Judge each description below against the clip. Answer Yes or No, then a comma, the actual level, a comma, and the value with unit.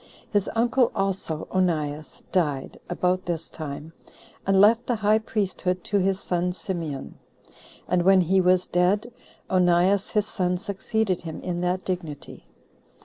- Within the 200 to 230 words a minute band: No, average, 140 wpm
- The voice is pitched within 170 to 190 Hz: Yes, medium, 185 Hz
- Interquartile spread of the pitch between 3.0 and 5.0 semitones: No, narrow, 2.5 semitones